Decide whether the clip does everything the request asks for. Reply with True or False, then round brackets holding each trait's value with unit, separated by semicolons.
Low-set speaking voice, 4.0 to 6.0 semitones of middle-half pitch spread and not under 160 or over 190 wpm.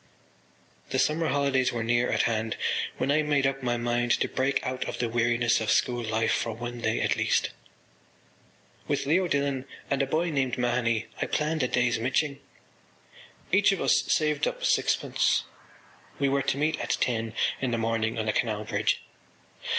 False (125 Hz; 3.2 semitones; 180 wpm)